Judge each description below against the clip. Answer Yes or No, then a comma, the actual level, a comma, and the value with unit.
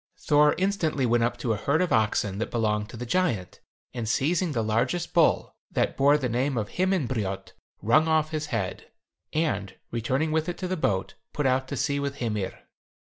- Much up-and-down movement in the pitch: Yes, wide, 5.8 semitones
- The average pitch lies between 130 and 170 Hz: Yes, low, 135 Hz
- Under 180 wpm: No, average, 190 wpm